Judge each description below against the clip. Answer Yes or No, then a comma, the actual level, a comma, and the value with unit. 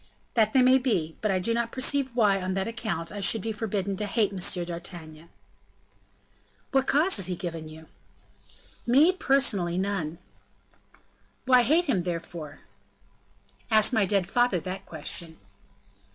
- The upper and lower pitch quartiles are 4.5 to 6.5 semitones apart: Yes, wide, 5.5 semitones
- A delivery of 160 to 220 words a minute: No, average, 150 wpm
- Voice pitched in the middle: No, high, 200 Hz